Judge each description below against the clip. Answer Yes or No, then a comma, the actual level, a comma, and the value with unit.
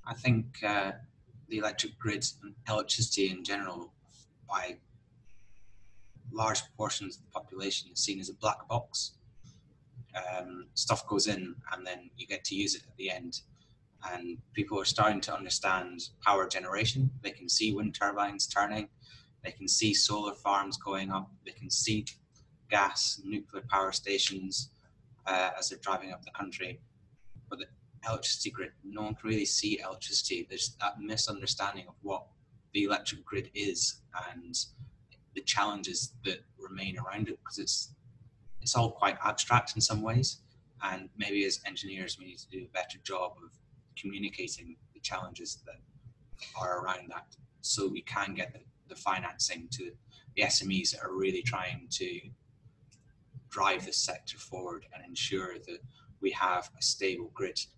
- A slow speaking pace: No, average, 160 wpm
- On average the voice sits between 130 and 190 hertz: No, low, 110 Hz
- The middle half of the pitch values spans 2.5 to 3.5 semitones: No, average, 4.3 semitones